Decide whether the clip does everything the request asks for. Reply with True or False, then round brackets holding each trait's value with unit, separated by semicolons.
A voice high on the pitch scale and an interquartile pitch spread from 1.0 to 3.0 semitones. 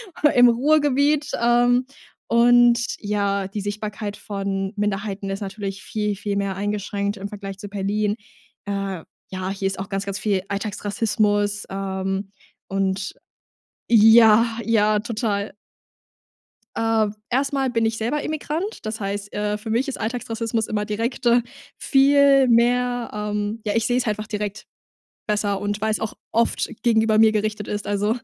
True (210 Hz; 2.7 semitones)